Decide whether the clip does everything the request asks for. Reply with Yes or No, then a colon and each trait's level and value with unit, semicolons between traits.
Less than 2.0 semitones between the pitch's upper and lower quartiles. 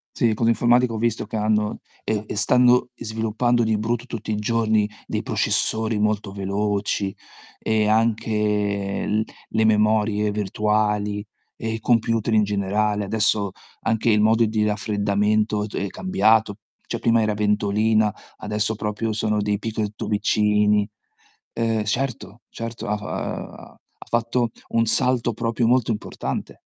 Yes: narrow, 1.3 semitones